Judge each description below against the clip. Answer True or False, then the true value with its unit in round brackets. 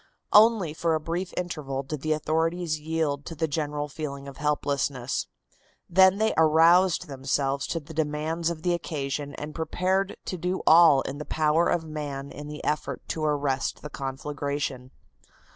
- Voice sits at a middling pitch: True (155 Hz)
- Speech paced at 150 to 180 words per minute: True (160 wpm)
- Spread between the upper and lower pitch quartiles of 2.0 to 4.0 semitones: True (2.7 semitones)